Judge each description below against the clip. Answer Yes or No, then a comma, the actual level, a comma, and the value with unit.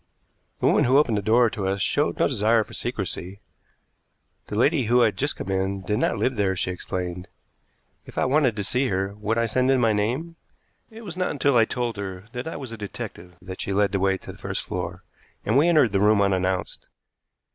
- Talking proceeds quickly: Yes, fast, 220 wpm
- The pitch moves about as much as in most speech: Yes, average, 4.8 semitones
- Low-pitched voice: Yes, low, 110 Hz